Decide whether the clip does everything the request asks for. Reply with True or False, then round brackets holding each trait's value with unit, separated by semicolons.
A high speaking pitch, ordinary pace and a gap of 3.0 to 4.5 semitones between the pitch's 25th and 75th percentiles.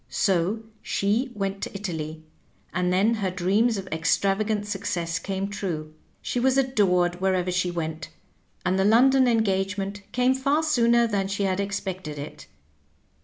True (195 Hz; 150 wpm; 3.5 semitones)